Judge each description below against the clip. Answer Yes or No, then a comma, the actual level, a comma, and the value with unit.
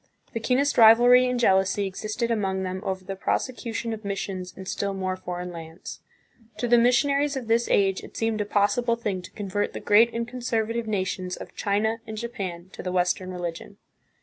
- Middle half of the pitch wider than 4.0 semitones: No, average, 3.7 semitones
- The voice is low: No, high, 205 Hz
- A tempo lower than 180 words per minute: No, average, 185 wpm